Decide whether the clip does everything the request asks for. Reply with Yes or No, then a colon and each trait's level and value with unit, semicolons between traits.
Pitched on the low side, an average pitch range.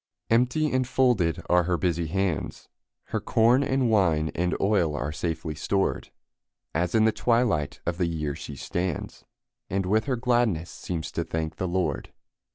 No: very low, 90 Hz; wide, 5.9 semitones